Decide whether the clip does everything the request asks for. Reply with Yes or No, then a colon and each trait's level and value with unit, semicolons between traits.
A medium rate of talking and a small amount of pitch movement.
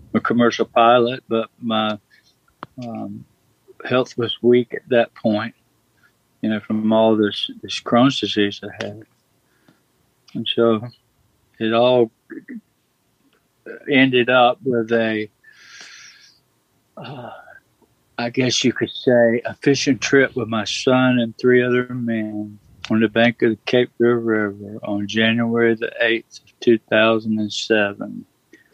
No: slow, 125 wpm; narrow, 2.1 semitones